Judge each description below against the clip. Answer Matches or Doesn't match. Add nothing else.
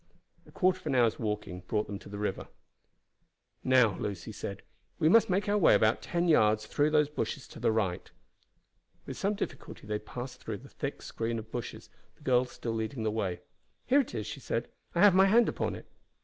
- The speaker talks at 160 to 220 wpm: Matches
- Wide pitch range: Matches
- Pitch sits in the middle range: Doesn't match